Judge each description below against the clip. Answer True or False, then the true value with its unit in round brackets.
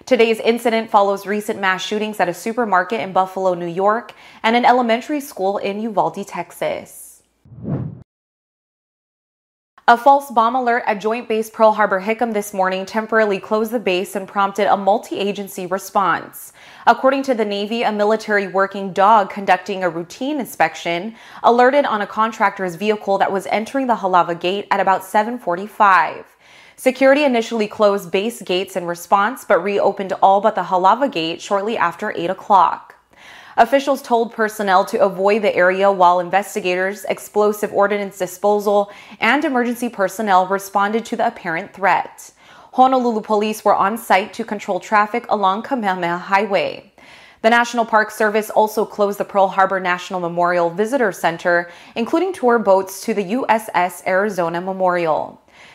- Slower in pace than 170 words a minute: True (145 wpm)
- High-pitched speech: True (205 Hz)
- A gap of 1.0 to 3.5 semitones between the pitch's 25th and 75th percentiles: True (2.9 semitones)